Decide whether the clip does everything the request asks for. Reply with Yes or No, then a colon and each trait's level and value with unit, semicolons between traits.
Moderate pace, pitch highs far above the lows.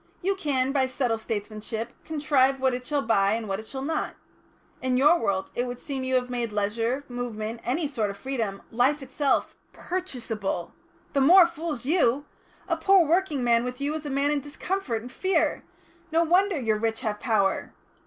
No: average, 185 wpm; average, 4.6 semitones